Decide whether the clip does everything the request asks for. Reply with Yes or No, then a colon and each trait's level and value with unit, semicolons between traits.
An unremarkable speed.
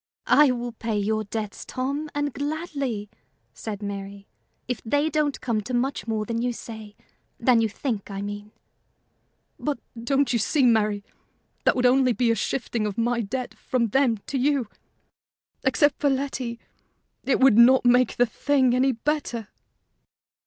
Yes: average, 160 wpm